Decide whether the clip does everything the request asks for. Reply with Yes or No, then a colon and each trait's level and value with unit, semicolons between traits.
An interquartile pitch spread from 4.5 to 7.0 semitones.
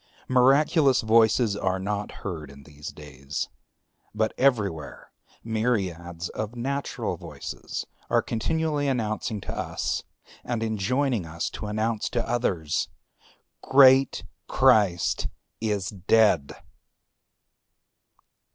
Yes: average, 5.2 semitones